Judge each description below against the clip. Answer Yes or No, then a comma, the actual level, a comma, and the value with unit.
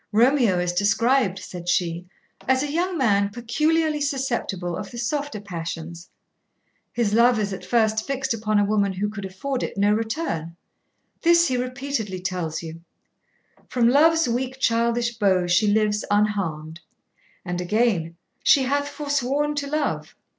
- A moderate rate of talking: Yes, average, 145 wpm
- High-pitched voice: Yes, high, 220 Hz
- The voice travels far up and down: Yes, wide, 6.0 semitones